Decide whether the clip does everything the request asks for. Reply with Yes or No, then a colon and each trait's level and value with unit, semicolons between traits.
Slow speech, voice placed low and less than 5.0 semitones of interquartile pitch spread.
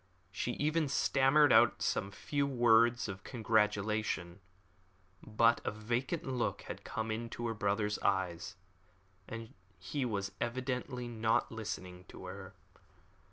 Yes: slow, 120 wpm; low, 115 Hz; average, 3.2 semitones